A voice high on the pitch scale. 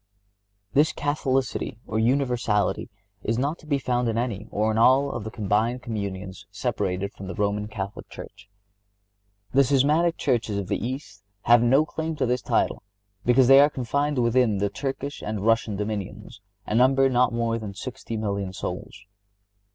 No: low, 115 Hz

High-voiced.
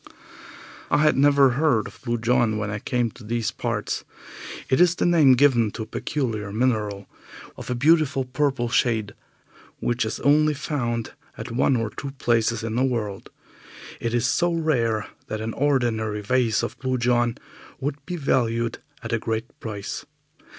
No: low, 120 Hz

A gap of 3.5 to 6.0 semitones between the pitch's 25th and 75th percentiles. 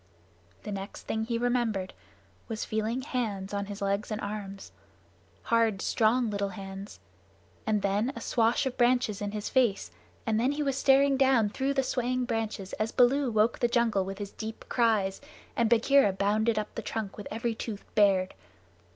No: average, 3.1 semitones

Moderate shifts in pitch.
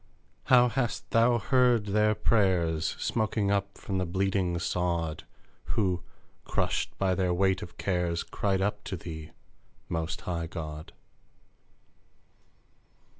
Yes: average, 3.6 semitones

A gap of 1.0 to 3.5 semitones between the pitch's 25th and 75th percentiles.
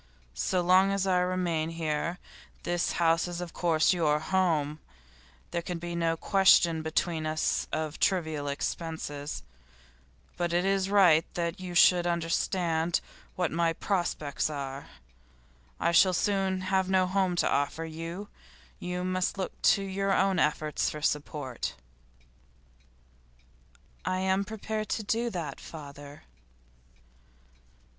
Yes: average, 2.9 semitones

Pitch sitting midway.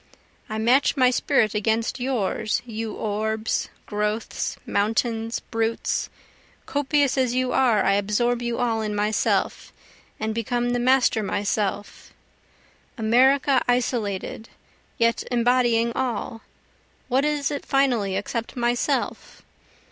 No: high, 230 Hz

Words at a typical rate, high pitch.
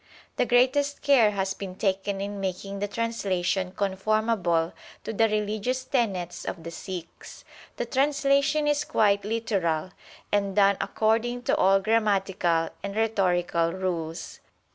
No: slow, 130 wpm; high, 200 Hz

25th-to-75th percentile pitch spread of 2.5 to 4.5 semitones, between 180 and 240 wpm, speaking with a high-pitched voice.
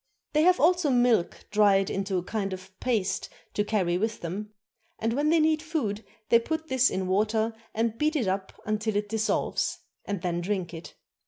No: average, 5.1 semitones; average, 185 wpm; high, 215 Hz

